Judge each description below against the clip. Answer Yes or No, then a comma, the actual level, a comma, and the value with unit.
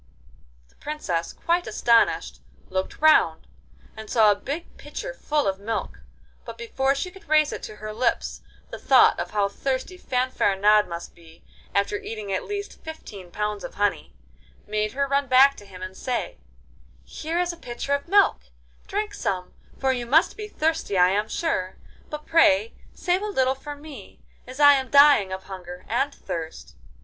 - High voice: Yes, very high, 255 Hz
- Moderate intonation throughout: No, wide, 7.2 semitones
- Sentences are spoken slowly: No, average, 175 wpm